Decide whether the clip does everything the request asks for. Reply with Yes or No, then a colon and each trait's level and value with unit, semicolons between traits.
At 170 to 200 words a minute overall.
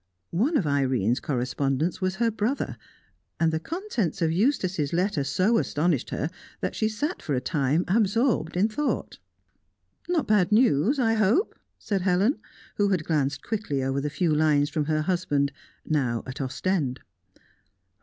No: average, 155 wpm